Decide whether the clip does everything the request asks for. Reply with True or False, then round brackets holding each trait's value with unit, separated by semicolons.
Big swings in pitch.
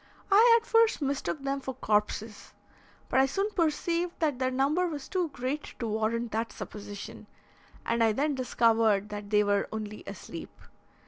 True (6.0 semitones)